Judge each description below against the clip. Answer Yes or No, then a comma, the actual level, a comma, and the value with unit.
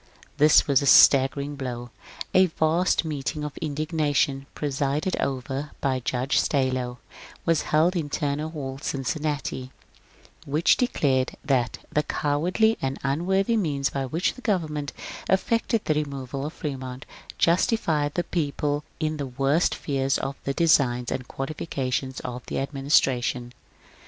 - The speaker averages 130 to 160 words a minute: Yes, slow, 135 wpm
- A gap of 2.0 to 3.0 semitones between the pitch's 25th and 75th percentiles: Yes, average, 2.7 semitones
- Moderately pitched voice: Yes, medium, 145 Hz